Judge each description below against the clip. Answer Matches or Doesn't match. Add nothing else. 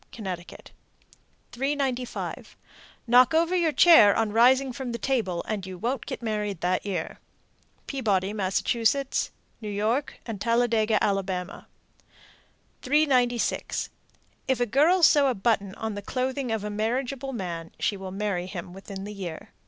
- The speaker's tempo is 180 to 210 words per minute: Doesn't match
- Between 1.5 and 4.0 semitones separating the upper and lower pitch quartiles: Doesn't match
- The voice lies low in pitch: Doesn't match